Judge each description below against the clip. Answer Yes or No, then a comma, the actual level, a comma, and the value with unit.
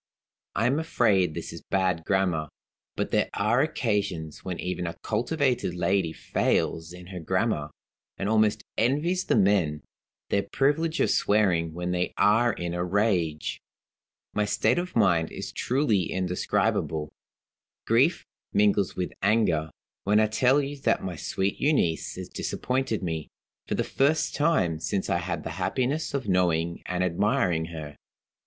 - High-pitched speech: No, very low, 95 Hz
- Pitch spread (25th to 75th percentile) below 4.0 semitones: No, wide, 5.4 semitones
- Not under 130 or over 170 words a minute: Yes, average, 150 wpm